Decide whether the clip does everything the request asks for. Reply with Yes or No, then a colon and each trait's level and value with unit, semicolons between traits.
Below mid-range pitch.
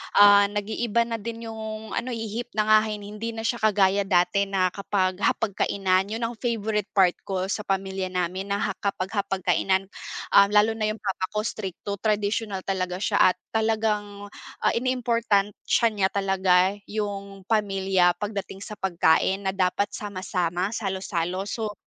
No: high, 200 Hz